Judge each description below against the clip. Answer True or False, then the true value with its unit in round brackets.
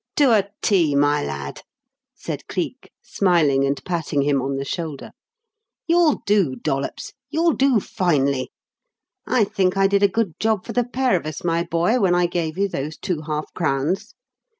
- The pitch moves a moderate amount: False (5.9 semitones)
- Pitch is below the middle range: False (175 Hz)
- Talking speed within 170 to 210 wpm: True (175 wpm)